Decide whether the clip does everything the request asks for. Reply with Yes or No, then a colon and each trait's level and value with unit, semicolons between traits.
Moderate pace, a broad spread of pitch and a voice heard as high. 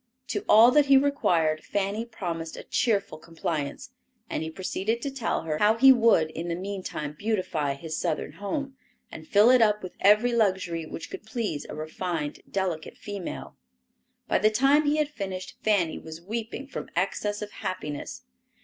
Yes: average, 170 wpm; wide, 5.8 semitones; high, 200 Hz